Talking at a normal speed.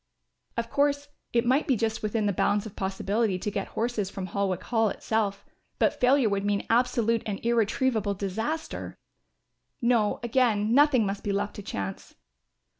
Yes: average, 160 wpm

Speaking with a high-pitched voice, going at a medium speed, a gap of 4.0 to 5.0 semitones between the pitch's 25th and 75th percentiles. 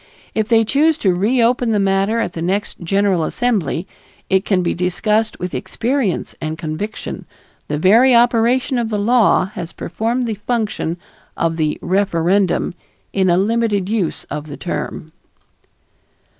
Yes: high, 200 Hz; average, 145 wpm; average, 4.5 semitones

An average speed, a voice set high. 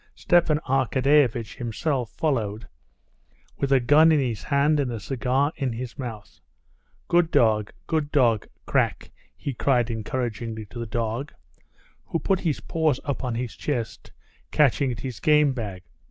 No: average, 150 wpm; low, 130 Hz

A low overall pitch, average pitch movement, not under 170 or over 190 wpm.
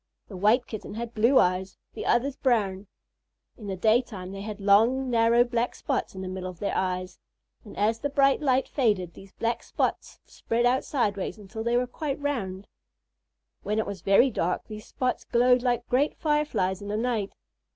No: high, 225 Hz; average, 4.1 semitones; average, 185 wpm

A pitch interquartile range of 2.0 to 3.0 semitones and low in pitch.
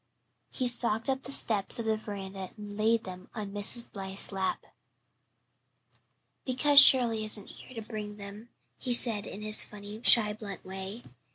No: narrow, 2.6 semitones; high, 215 Hz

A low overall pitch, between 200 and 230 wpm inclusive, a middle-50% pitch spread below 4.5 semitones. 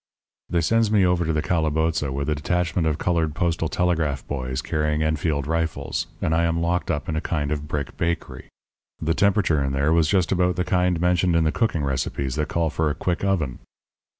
Yes: very low, 80 Hz; fast, 205 wpm; average, 2.8 semitones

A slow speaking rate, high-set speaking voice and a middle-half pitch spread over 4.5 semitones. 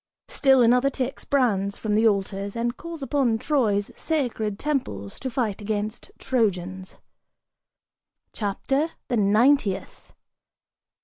Yes: slow, 110 wpm; high, 225 Hz; average, 4.9 semitones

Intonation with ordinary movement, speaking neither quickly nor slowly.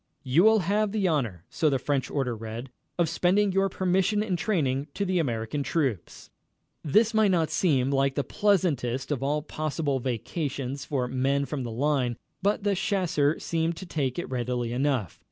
No: wide, 5.9 semitones; average, 175 wpm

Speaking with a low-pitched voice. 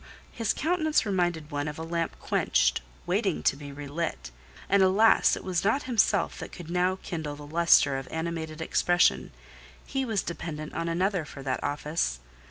No: medium, 165 Hz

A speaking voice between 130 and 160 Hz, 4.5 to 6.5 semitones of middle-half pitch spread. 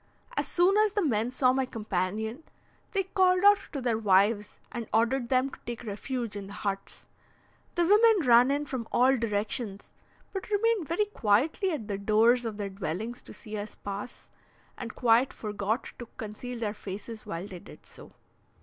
No: high, 235 Hz; average, 5.0 semitones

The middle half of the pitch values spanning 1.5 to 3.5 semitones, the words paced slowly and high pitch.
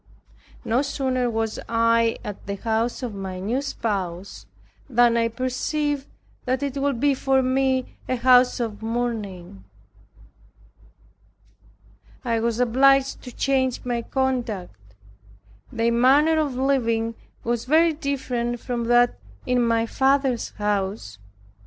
Yes: average, 2.7 semitones; slow, 120 wpm; high, 240 Hz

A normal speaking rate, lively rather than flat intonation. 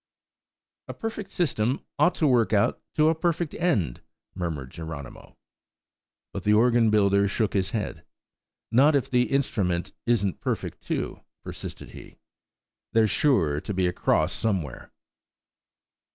No: slow, 130 wpm; wide, 7.2 semitones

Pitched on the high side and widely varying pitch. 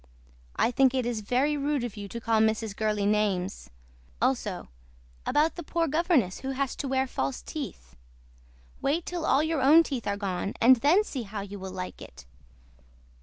Yes: high, 240 Hz; wide, 6.1 semitones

